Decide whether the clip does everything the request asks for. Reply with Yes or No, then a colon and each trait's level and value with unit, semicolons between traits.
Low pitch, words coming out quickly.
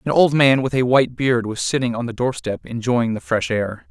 Yes: low, 125 Hz; fast, 245 wpm